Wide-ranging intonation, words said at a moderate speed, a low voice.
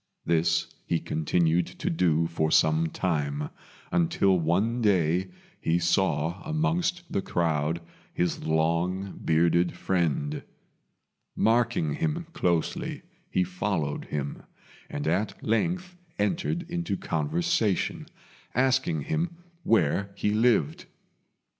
No: wide, 6.3 semitones; slow, 105 wpm; very low, 90 Hz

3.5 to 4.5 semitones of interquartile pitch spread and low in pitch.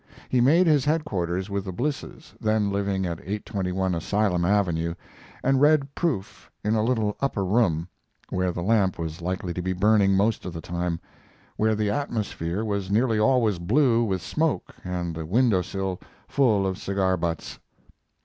Yes: average, 4.0 semitones; low, 100 Hz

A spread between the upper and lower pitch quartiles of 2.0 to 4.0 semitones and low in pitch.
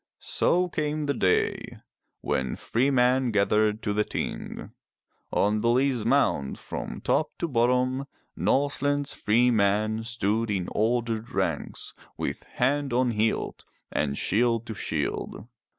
Yes: average, 3.7 semitones; low, 115 Hz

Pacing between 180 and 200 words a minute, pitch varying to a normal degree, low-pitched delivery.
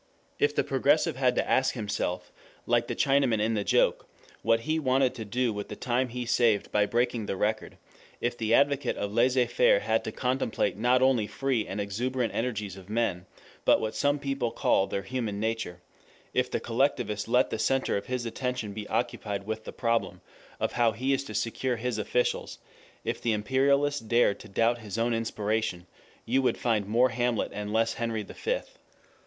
Yes: average, 190 wpm; average, 3.2 semitones; low, 115 Hz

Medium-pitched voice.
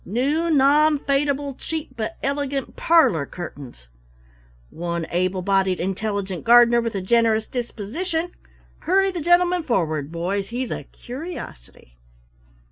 No: high, 235 Hz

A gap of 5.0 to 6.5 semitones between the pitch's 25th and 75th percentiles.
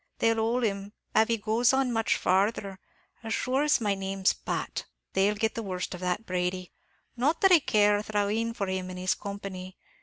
No: average, 3.2 semitones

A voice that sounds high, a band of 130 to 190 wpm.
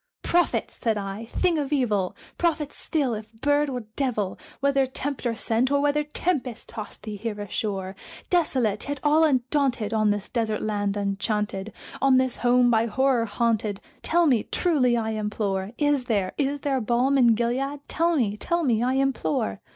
Yes: high, 245 Hz; average, 165 wpm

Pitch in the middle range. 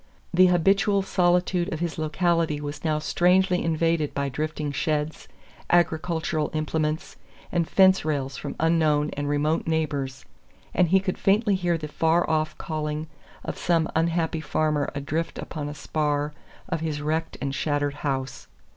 Yes: medium, 155 Hz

